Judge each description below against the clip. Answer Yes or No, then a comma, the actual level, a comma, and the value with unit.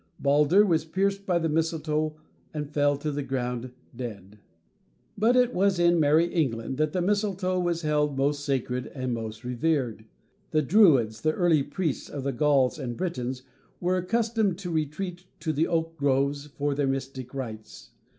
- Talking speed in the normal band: Yes, average, 160 wpm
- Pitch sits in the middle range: Yes, medium, 150 Hz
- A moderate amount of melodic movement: Yes, average, 4.5 semitones